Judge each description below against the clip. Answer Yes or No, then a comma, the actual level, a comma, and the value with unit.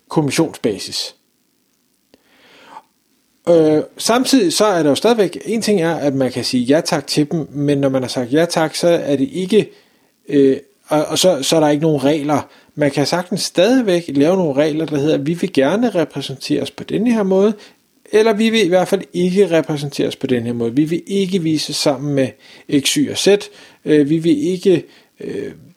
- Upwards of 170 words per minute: Yes, average, 200 wpm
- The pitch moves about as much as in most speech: No, wide, 5.7 semitones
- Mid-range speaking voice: Yes, medium, 160 Hz